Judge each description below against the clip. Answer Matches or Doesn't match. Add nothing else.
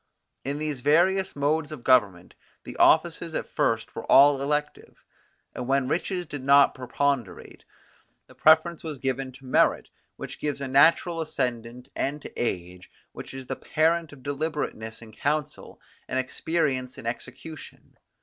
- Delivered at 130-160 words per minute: Matches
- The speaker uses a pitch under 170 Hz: Matches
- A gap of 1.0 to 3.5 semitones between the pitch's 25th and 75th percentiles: Matches